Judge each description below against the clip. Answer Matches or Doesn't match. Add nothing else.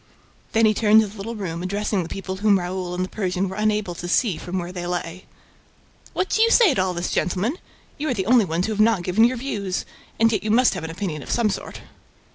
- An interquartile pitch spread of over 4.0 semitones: Doesn't match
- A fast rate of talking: Matches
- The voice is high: Matches